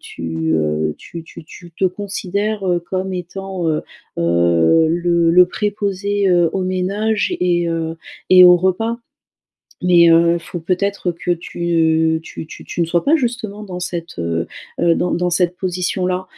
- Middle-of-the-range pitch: Yes, medium, 175 Hz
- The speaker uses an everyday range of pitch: No, narrow, 2.3 semitones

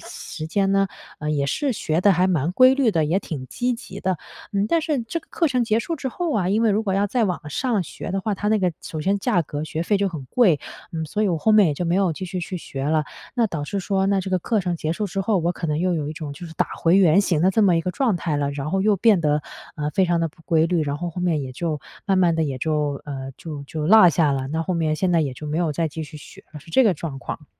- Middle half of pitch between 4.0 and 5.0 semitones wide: Yes, average, 4.6 semitones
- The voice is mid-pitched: Yes, medium, 175 Hz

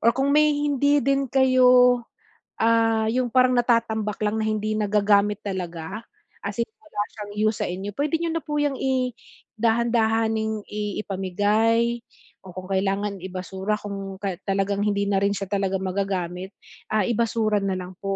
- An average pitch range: Yes, average, 3.2 semitones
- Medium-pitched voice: No, high, 215 Hz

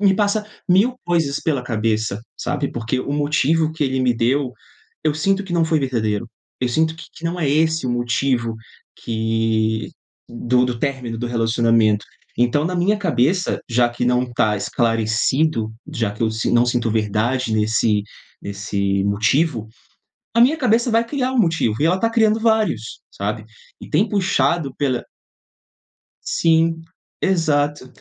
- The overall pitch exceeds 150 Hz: No, low, 130 Hz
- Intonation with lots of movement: Yes, wide, 6.4 semitones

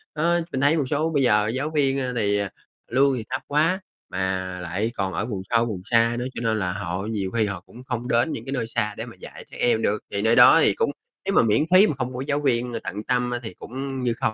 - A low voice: Yes, low, 120 Hz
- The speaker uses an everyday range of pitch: Yes, average, 4.3 semitones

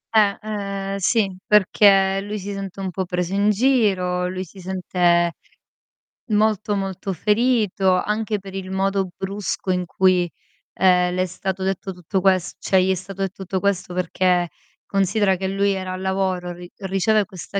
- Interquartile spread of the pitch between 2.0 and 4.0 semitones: No, narrow, 1.5 semitones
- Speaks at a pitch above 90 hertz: Yes, high, 190 Hz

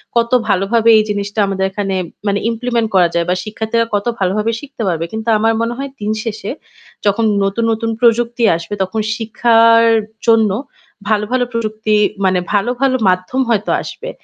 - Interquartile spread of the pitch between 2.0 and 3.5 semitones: Yes, narrow, 2.4 semitones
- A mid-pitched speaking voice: No, high, 220 Hz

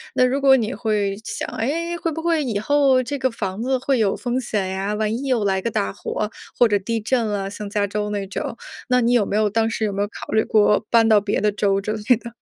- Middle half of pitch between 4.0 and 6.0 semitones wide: No, average, 3.6 semitones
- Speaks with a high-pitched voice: Yes, high, 220 Hz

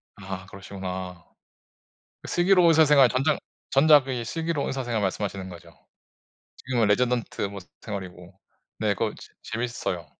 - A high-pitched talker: No, low, 110 Hz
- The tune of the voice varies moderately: No, wide, 6.1 semitones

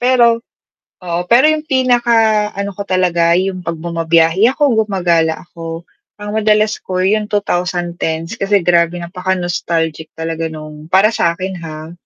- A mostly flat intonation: No, average, 4.0 semitones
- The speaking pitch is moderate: Yes, medium, 180 Hz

